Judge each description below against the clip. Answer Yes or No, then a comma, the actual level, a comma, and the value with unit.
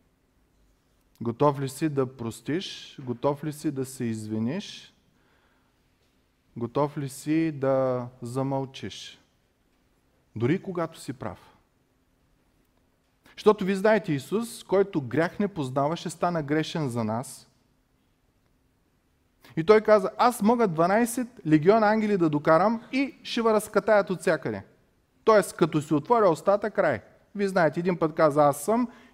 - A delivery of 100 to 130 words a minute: Yes, average, 125 wpm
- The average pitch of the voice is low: No, medium, 165 Hz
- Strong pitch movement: Yes, wide, 7.0 semitones